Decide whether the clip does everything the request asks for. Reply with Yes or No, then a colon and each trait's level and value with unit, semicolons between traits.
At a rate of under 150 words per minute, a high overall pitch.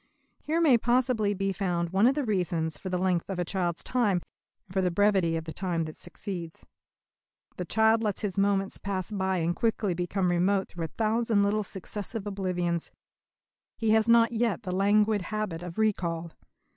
No: average, 185 wpm; high, 195 Hz